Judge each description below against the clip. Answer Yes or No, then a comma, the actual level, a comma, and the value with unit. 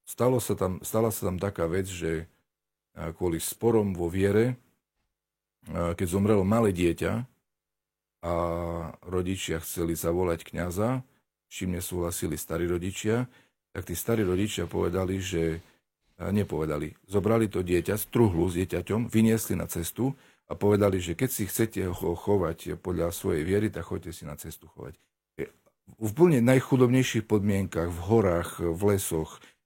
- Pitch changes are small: No, average, 4.2 semitones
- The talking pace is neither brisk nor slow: Yes, average, 135 wpm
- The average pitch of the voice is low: Yes, very low, 95 Hz